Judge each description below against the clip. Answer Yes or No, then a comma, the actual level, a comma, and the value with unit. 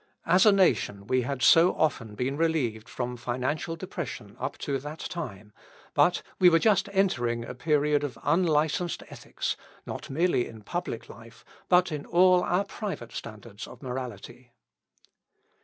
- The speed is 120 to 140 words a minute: No, average, 150 wpm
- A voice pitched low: No, medium, 145 Hz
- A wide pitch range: Yes, wide, 6.4 semitones